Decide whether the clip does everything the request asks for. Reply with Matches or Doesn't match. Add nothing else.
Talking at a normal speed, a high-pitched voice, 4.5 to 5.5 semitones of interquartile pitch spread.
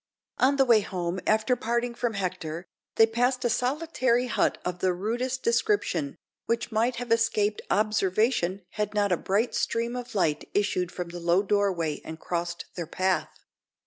Matches